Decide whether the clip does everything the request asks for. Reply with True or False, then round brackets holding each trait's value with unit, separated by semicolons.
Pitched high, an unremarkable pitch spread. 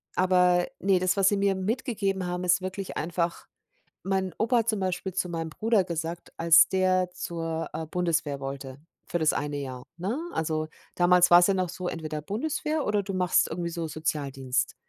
False (180 Hz; 3.0 semitones)